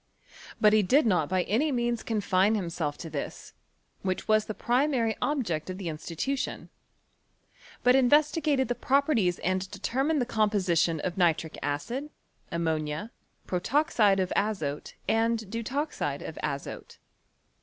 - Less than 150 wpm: Yes, slow, 135 wpm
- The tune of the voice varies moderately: No, wide, 6.0 semitones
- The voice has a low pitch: No, high, 215 Hz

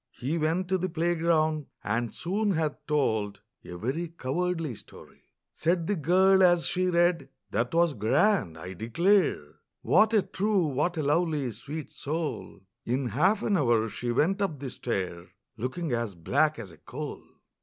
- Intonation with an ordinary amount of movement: No, wide, 6.7 semitones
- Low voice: No, medium, 155 Hz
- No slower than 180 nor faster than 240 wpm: No, average, 160 wpm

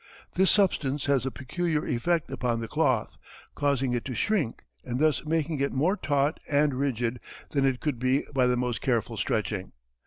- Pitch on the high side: No, low, 135 Hz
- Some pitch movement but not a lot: Yes, average, 3.5 semitones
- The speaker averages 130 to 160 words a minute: No, average, 180 wpm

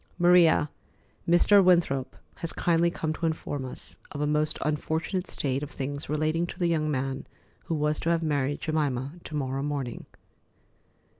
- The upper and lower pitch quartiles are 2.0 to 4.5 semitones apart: Yes, average, 2.8 semitones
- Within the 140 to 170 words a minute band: Yes, average, 160 wpm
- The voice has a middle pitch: Yes, medium, 150 Hz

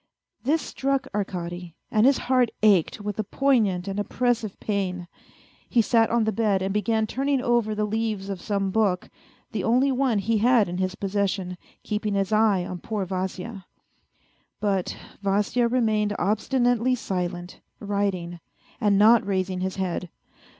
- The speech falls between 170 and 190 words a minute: No, average, 150 wpm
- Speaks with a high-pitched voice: Yes, high, 205 Hz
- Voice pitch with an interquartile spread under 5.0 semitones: Yes, average, 3.3 semitones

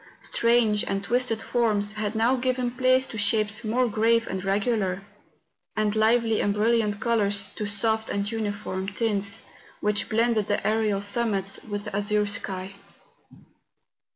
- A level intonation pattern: Yes, narrow, 2.2 semitones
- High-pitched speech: Yes, high, 215 Hz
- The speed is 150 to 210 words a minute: No, average, 140 wpm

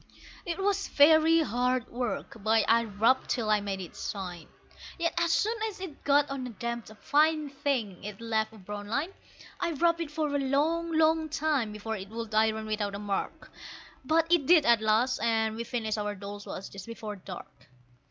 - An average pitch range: No, wide, 6.4 semitones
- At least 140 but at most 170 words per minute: No, average, 190 wpm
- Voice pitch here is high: Yes, high, 235 Hz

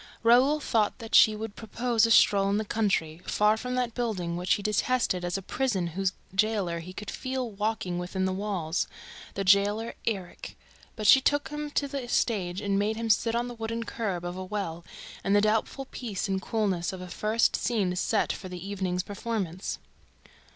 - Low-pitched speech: No, high, 210 Hz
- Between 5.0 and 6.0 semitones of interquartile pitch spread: No, average, 3.6 semitones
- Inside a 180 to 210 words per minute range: Yes, average, 195 wpm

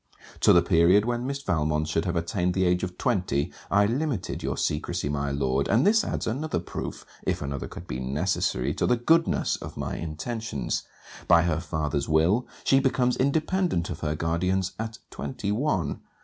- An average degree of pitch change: No, wide, 7.7 semitones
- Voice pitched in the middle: No, very low, 90 Hz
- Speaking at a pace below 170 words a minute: No, average, 175 wpm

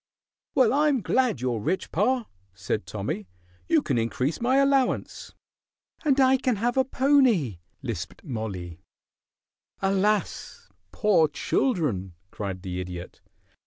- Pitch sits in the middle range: Yes, medium, 180 Hz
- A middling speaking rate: No, slow, 125 wpm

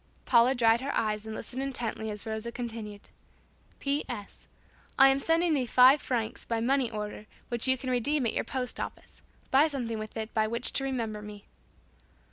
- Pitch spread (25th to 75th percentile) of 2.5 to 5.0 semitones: Yes, average, 3.4 semitones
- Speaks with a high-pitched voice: Yes, high, 235 Hz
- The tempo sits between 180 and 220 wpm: Yes, average, 185 wpm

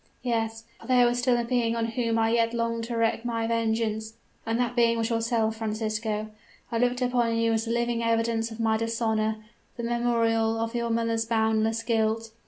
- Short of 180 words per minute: No, average, 190 wpm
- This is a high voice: Yes, high, 230 Hz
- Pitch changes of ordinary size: No, narrow, 0.8 semitones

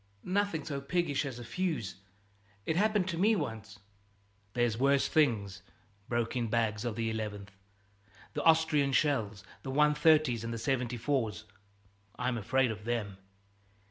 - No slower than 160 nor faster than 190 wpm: No, average, 140 wpm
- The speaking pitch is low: Yes, low, 120 Hz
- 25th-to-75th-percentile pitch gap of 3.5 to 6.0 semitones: Yes, wide, 5.4 semitones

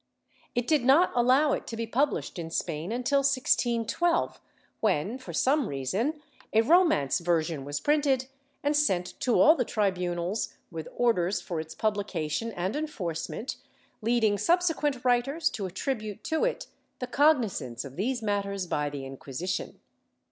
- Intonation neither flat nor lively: No, wide, 7.7 semitones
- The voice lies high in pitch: Yes, high, 225 Hz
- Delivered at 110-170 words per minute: Yes, average, 150 wpm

